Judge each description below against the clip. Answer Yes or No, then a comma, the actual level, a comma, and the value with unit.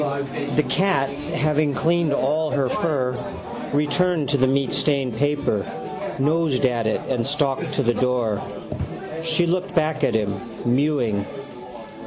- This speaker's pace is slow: Yes, slow, 130 wpm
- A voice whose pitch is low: No, medium, 145 Hz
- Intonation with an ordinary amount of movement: Yes, average, 3.5 semitones